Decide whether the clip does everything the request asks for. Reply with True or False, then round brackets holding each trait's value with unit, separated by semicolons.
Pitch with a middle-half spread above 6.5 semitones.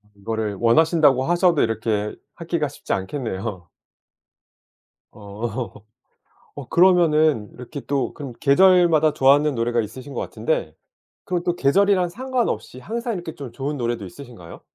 True (6.9 semitones)